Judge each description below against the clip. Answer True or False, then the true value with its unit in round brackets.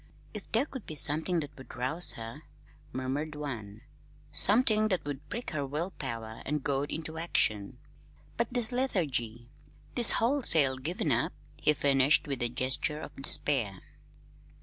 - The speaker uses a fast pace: False (150 wpm)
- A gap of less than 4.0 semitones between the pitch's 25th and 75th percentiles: False (5.2 semitones)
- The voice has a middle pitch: True (145 Hz)